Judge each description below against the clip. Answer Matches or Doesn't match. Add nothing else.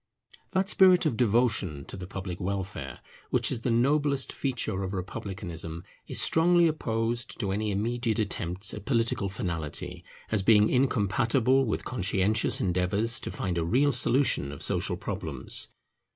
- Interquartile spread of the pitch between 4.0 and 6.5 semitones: Matches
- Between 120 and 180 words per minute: Matches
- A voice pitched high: Doesn't match